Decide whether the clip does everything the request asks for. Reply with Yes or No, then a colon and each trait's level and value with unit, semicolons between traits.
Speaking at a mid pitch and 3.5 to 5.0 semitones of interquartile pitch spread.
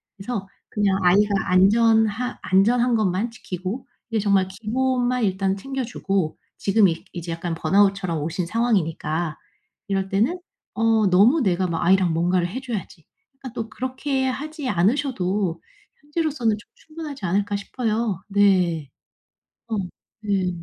No: high, 205 Hz; average, 4.6 semitones